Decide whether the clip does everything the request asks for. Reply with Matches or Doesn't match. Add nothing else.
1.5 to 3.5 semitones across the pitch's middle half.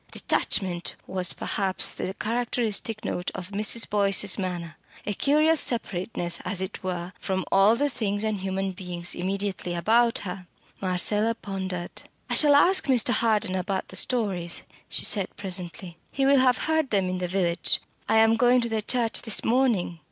Doesn't match